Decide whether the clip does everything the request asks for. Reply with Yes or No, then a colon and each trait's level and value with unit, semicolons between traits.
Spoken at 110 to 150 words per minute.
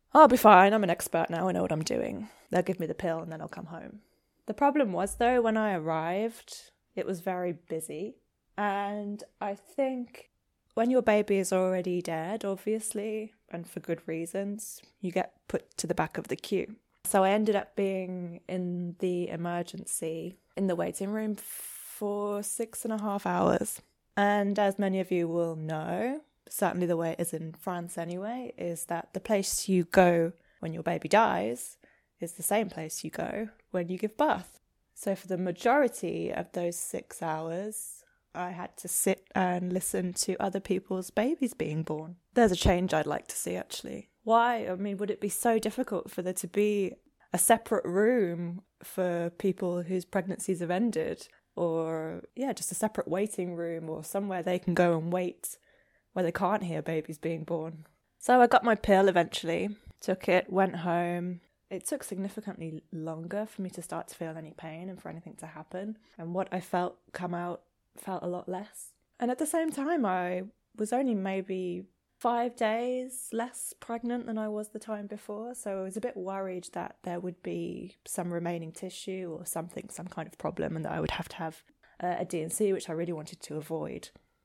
No: average, 190 wpm